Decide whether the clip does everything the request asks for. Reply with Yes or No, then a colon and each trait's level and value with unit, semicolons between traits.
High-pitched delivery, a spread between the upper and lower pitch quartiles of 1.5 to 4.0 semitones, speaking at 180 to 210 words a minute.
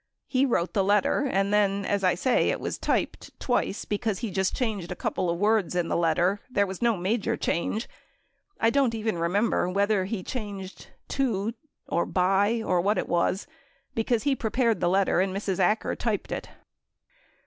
Yes: high, 200 Hz; average, 3.3 semitones; average, 185 wpm